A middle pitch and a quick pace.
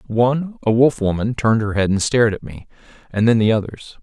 No: low, 110 Hz; fast, 225 wpm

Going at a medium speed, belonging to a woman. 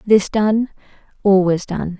Yes: average, 150 wpm; female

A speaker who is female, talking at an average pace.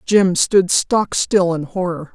Yes: female; average, 170 wpm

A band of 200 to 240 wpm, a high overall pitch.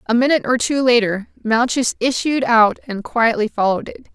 No: average, 175 wpm; high, 235 Hz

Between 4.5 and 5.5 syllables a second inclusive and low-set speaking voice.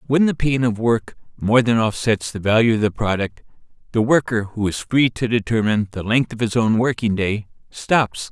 Yes: 5.0 syllables/s; low, 115 Hz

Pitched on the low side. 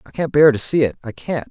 Yes: low, 130 Hz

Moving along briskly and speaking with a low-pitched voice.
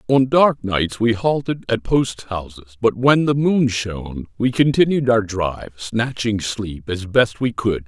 No: average, 175 wpm; low, 115 Hz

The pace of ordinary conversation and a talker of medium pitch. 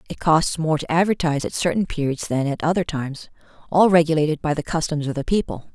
No: fast, 210 wpm; medium, 160 Hz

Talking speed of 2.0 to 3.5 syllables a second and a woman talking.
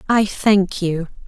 Yes: 3.2 syllables/s; female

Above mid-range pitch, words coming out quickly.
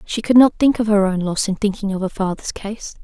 Yes: high, 205 Hz; fast, 275 wpm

